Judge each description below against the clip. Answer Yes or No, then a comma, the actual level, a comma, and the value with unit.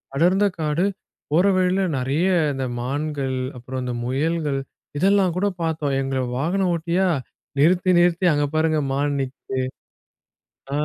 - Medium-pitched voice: Yes, medium, 155 Hz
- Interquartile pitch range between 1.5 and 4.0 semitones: No, average, 4.8 semitones